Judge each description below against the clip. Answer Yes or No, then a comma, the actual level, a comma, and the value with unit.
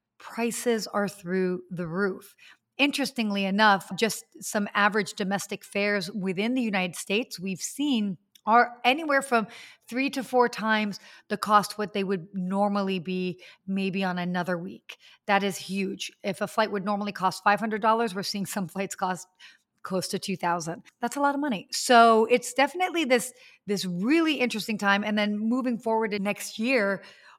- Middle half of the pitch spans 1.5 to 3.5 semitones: Yes, average, 3.2 semitones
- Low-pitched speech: No, high, 205 Hz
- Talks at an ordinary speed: Yes, average, 160 wpm